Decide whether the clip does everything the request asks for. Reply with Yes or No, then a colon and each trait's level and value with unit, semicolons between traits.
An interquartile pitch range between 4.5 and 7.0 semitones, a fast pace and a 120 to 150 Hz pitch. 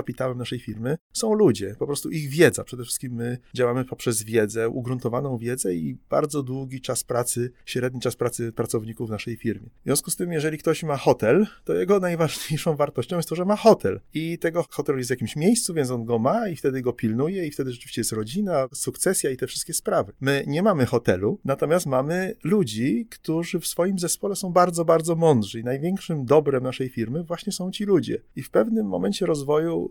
Yes: wide, 5.6 semitones; fast, 200 wpm; medium, 140 Hz